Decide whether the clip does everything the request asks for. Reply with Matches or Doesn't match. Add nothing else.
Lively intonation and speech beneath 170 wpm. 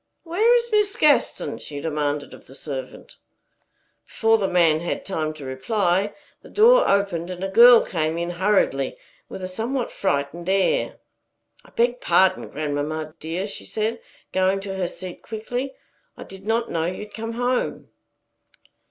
Matches